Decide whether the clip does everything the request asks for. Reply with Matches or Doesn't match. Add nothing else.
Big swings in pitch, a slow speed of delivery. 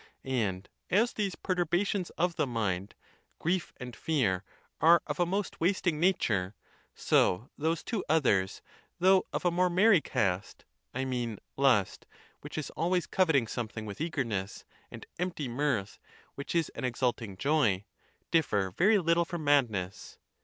Doesn't match